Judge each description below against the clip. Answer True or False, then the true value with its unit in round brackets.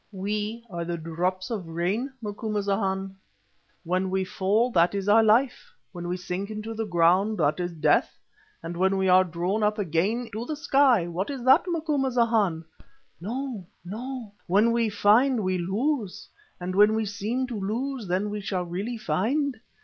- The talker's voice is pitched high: True (205 Hz)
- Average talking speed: True (165 wpm)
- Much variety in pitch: False (4.1 semitones)